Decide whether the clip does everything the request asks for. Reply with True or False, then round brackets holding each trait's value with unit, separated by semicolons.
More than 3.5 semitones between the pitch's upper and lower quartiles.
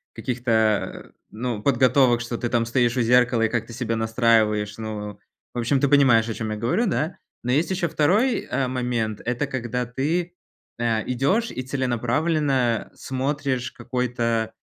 False (2.8 semitones)